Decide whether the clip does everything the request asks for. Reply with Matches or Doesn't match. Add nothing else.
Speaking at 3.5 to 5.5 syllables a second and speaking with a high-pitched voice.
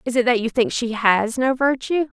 Matches